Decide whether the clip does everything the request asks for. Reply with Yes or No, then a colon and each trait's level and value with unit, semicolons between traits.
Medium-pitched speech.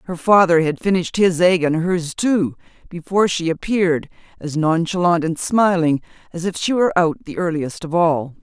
Yes: medium, 170 Hz